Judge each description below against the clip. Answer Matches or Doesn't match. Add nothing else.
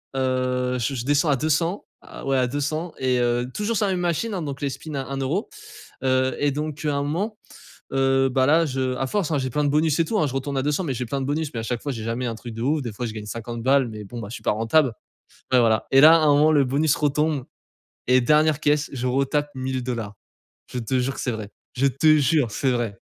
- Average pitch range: Matches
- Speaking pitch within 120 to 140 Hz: Matches